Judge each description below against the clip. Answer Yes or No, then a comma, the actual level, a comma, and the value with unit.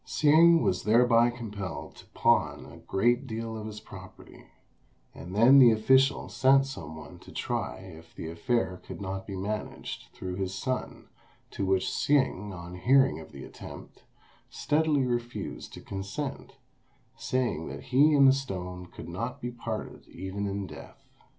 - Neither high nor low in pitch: No, low, 110 Hz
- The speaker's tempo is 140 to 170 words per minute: Yes, average, 155 wpm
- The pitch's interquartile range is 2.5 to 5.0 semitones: No, wide, 5.6 semitones